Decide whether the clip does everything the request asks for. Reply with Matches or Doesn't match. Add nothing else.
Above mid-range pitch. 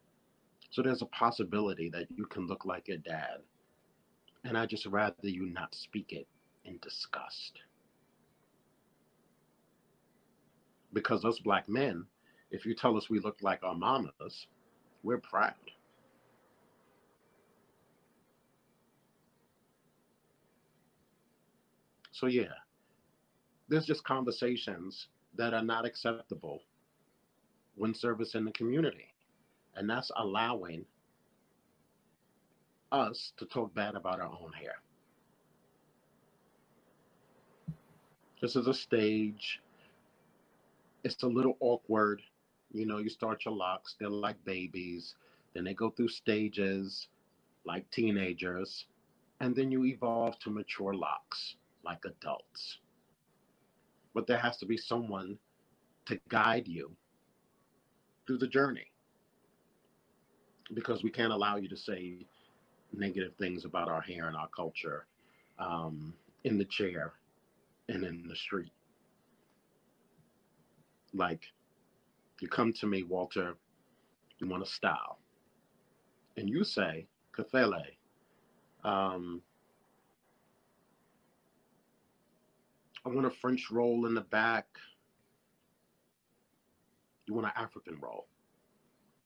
Doesn't match